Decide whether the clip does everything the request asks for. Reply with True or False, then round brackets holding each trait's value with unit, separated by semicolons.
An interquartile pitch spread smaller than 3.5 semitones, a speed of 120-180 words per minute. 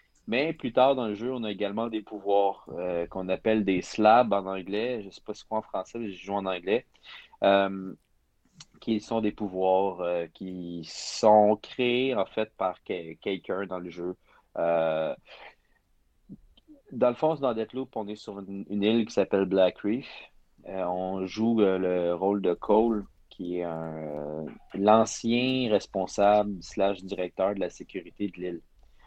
True (3.1 semitones; 175 wpm)